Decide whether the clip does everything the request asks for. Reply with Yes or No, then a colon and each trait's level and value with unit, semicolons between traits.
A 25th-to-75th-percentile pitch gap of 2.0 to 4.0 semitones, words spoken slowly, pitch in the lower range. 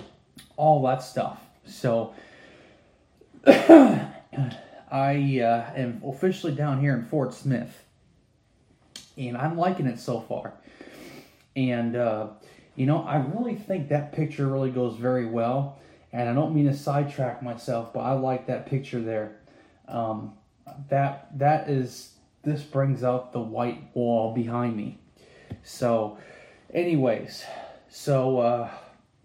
Yes: average, 3.1 semitones; slow, 125 wpm; low, 130 Hz